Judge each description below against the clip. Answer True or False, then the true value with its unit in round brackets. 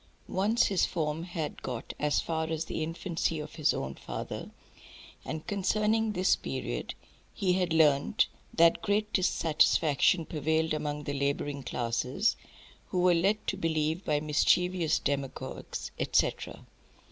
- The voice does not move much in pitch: False (3.6 semitones)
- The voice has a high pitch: False (160 Hz)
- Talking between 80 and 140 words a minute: True (135 wpm)